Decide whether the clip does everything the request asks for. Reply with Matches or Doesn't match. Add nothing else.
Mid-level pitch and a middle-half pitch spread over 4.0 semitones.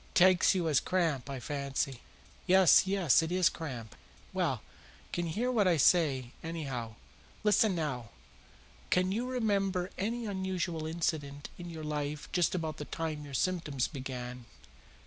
Matches